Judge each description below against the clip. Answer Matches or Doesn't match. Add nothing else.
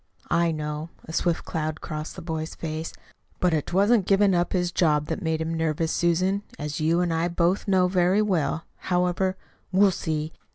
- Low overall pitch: Doesn't match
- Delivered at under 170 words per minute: Doesn't match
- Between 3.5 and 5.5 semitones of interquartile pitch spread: Doesn't match